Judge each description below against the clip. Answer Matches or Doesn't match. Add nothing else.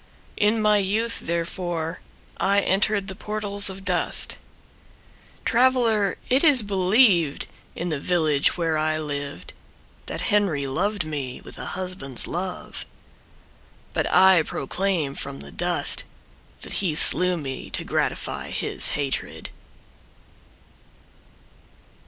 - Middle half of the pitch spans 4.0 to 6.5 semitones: Matches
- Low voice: Doesn't match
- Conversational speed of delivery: Doesn't match